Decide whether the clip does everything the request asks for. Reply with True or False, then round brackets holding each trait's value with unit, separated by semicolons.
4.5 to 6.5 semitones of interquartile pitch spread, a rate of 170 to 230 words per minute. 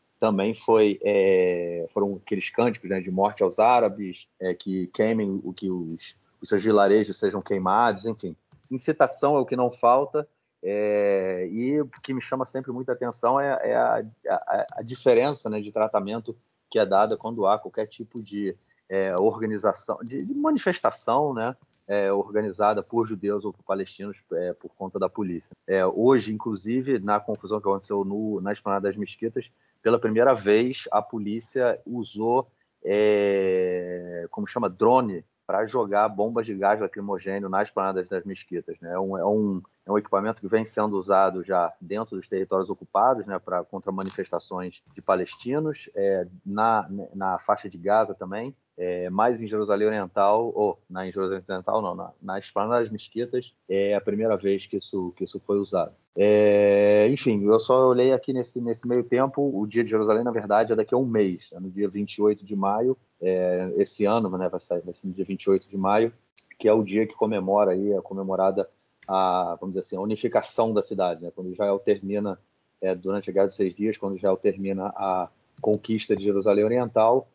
False (2.9 semitones; 185 wpm)